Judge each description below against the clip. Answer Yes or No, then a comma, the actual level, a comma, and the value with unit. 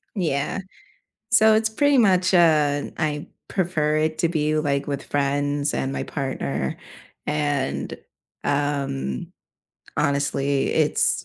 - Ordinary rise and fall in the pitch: Yes, average, 3.1 semitones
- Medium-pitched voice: Yes, medium, 145 Hz